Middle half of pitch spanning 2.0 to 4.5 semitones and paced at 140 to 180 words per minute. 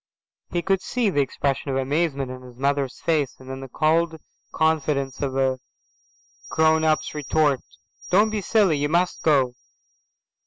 Yes: average, 3.4 semitones; average, 155 wpm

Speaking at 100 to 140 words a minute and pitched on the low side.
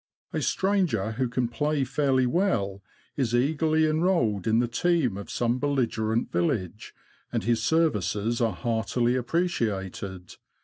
Yes: slow, 135 wpm; low, 120 Hz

